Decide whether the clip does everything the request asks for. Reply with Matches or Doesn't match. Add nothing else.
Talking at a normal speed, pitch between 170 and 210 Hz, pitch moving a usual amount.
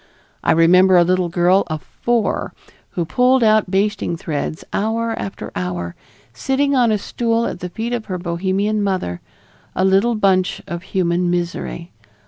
Matches